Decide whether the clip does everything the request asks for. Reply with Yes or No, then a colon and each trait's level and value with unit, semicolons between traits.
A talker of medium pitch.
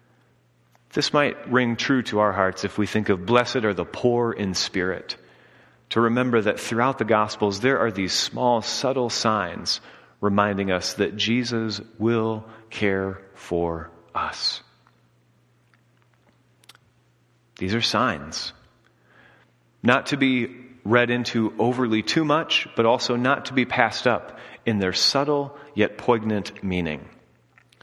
No: low, 110 Hz